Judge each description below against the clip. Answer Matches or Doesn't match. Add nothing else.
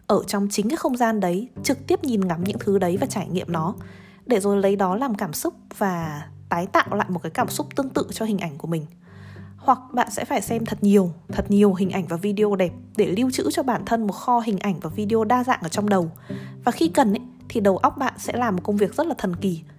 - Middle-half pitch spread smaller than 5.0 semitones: Matches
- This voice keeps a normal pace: Doesn't match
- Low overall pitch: Doesn't match